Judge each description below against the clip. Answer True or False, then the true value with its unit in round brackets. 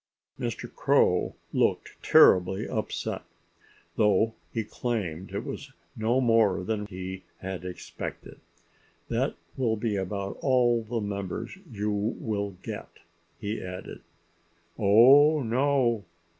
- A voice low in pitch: True (105 Hz)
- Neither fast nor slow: False (110 wpm)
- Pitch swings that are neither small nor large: True (3.2 semitones)